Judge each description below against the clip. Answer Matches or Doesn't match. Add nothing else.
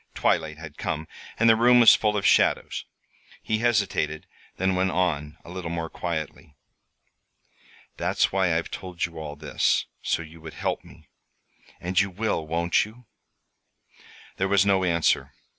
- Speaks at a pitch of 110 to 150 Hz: Doesn't match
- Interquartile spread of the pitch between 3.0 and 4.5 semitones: Matches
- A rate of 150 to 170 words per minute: Matches